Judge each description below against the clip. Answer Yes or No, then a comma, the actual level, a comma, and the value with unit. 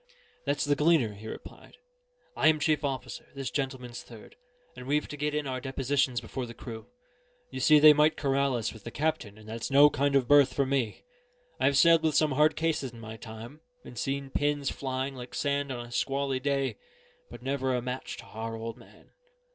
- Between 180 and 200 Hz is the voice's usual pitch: No, low, 135 Hz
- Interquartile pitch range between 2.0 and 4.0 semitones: Yes, average, 3.0 semitones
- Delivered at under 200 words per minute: No, fast, 205 wpm